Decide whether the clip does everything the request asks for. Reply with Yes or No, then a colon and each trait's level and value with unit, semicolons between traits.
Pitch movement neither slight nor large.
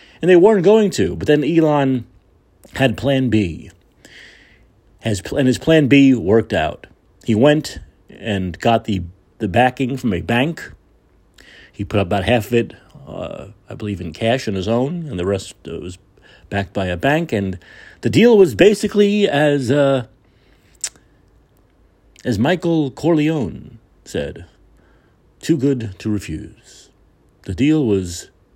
No: wide, 6.7 semitones